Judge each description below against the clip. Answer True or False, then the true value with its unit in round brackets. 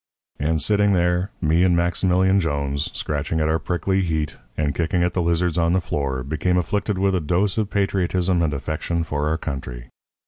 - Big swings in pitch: False (3.3 semitones)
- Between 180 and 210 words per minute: True (185 wpm)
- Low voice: True (85 Hz)